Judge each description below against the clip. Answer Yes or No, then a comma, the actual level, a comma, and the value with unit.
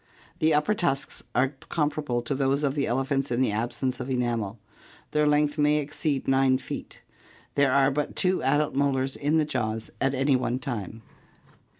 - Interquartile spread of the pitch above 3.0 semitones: No, narrow, 2.5 semitones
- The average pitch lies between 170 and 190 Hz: No, low, 135 Hz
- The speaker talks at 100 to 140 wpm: No, average, 175 wpm